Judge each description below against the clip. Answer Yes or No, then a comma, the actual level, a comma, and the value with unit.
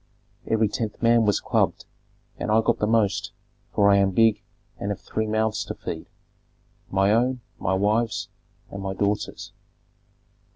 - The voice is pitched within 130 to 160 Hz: No, low, 105 Hz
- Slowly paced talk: No, average, 155 wpm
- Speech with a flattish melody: Yes, narrow, 2.0 semitones